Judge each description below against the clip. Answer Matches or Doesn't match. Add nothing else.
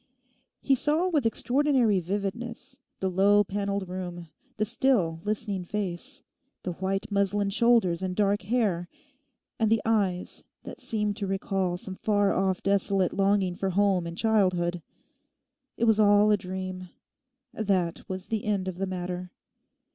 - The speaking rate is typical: Matches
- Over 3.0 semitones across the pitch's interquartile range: Doesn't match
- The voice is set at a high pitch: Matches